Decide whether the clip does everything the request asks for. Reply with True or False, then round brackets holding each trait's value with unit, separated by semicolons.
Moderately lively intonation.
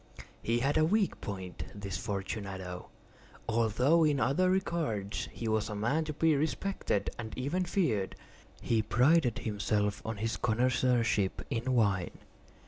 False (6.3 semitones)